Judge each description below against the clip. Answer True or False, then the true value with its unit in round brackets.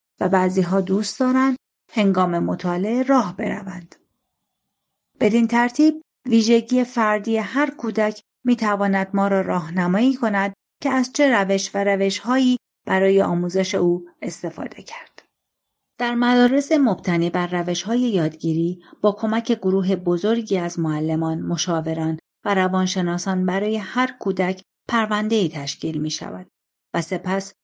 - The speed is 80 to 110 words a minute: False (130 wpm)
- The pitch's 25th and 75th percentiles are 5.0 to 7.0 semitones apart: False (4.4 semitones)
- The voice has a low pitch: False (195 Hz)